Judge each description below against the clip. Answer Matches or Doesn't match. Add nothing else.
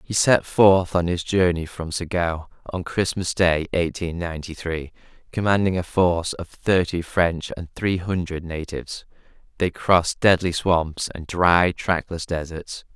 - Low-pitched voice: Matches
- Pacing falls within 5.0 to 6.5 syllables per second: Doesn't match